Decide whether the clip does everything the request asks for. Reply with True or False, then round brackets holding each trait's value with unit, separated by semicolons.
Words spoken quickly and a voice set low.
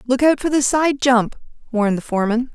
False (210 wpm; 250 Hz)